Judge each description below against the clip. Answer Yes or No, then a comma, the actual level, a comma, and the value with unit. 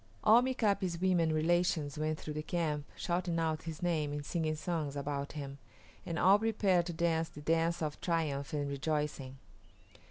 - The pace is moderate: Yes, average, 165 wpm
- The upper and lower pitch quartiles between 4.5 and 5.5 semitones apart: No, average, 2.7 semitones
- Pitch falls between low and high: Yes, medium, 160 Hz